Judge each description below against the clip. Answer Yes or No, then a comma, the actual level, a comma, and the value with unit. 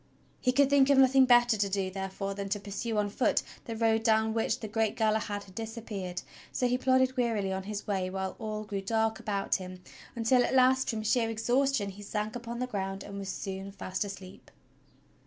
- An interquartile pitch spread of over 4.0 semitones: No, average, 3.4 semitones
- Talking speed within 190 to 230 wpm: Yes, fast, 205 wpm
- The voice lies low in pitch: No, high, 215 Hz